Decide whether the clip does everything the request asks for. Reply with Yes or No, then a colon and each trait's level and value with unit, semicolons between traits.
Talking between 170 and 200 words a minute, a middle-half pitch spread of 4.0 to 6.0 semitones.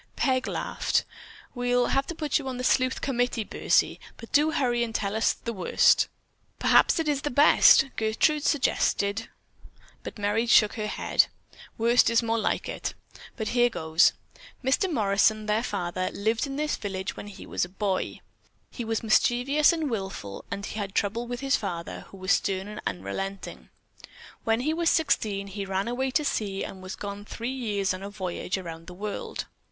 Yes: average, 180 wpm; average, 4.3 semitones